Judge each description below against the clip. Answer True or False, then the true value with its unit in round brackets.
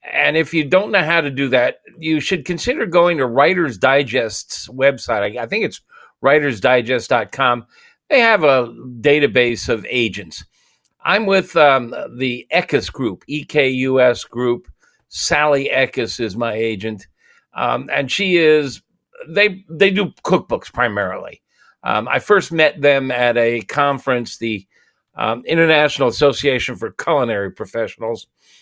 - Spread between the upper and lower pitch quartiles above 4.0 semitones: True (5.4 semitones)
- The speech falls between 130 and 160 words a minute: True (140 wpm)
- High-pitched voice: False (140 Hz)